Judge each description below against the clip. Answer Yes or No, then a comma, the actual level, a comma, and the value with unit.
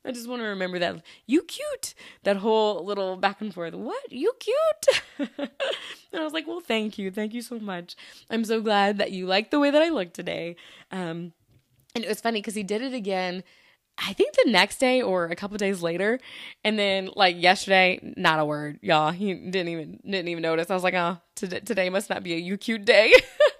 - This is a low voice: No, high, 200 Hz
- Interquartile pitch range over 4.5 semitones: Yes, average, 5.0 semitones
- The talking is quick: Yes, fast, 225 wpm